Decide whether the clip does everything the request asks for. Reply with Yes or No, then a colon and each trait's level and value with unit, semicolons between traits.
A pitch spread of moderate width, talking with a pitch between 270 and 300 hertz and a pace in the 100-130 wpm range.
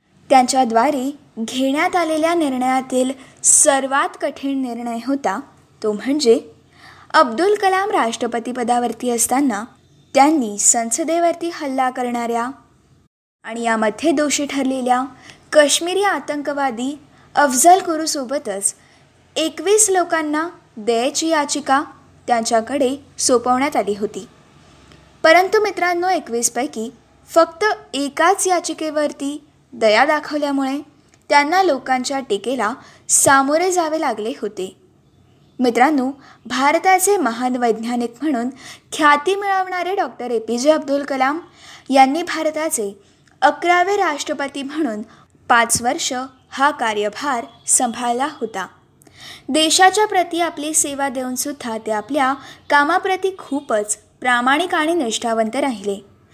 No: average, 4.8 semitones; very high, 280 Hz; average, 90 wpm